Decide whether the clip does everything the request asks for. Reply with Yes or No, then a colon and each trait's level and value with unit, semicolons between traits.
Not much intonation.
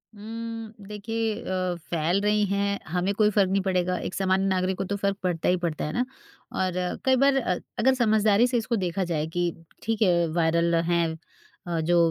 No: average, 3.5 semitones